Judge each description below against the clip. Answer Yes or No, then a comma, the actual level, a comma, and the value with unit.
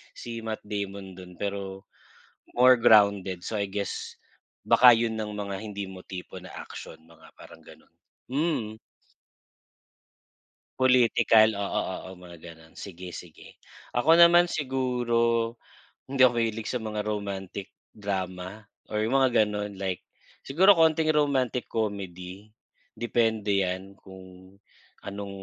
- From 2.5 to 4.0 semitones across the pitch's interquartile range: Yes, average, 3.7 semitones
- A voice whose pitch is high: No, low, 105 Hz